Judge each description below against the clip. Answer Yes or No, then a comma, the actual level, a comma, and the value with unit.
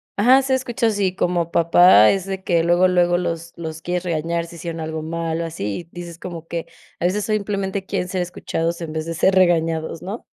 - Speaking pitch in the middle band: Yes, medium, 175 Hz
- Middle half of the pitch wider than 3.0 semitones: No, narrow, 2.4 semitones